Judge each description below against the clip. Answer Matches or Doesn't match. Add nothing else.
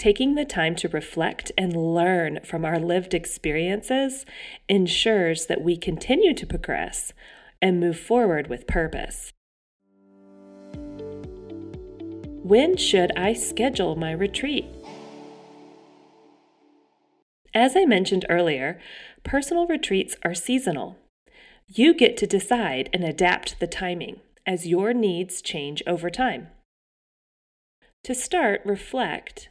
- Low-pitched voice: Doesn't match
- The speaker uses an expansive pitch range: Matches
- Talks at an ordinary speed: Doesn't match